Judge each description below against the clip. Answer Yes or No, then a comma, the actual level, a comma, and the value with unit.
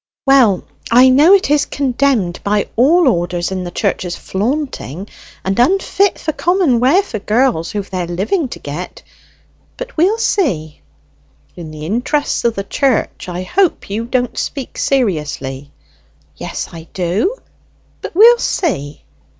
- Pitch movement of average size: No, wide, 8.5 semitones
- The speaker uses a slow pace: No, average, 145 wpm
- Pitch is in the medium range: No, high, 235 Hz